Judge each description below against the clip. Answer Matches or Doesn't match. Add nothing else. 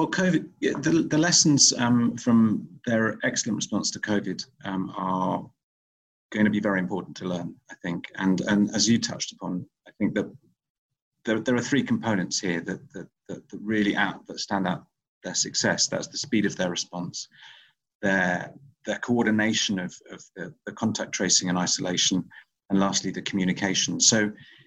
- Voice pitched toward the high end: Doesn't match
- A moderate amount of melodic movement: Matches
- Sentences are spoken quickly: Doesn't match